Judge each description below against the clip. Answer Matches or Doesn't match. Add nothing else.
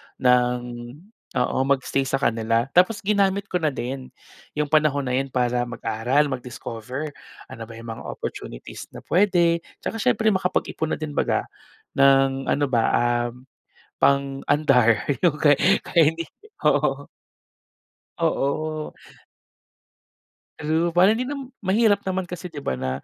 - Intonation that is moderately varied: Doesn't match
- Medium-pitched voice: Matches